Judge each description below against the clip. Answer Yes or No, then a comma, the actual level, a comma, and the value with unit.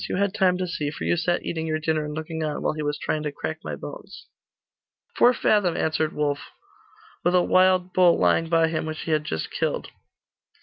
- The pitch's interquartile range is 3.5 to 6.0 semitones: No, average, 2.7 semitones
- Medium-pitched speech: Yes, medium, 160 Hz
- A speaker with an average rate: No, fast, 215 wpm